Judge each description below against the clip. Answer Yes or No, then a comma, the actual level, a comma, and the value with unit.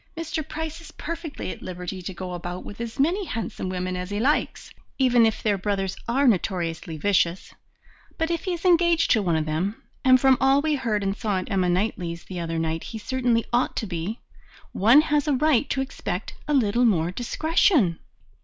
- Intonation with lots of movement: Yes, wide, 7.5 semitones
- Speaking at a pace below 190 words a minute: No, average, 200 wpm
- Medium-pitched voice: No, high, 220 Hz